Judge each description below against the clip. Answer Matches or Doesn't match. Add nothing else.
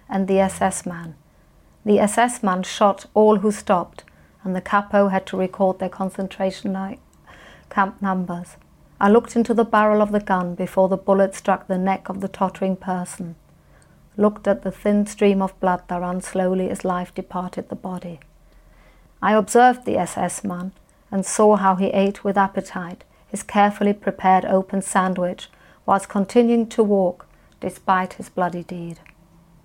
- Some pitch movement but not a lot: Doesn't match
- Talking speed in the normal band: Matches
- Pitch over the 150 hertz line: Matches